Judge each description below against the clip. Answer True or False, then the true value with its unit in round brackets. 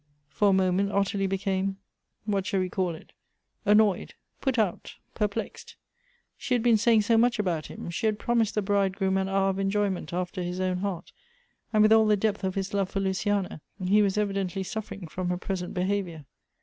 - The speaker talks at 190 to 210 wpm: True (200 wpm)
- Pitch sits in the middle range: False (195 Hz)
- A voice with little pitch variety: True (2.0 semitones)